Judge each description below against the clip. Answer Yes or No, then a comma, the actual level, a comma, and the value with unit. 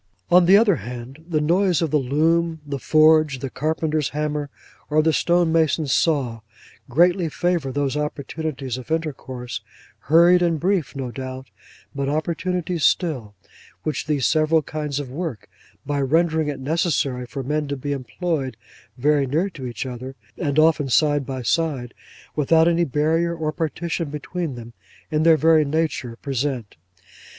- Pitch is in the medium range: Yes, medium, 150 Hz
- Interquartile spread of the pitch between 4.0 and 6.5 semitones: No, average, 3.4 semitones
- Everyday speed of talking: Yes, average, 145 wpm